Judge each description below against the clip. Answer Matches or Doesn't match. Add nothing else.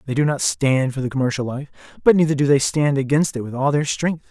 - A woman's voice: Doesn't match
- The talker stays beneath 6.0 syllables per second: Doesn't match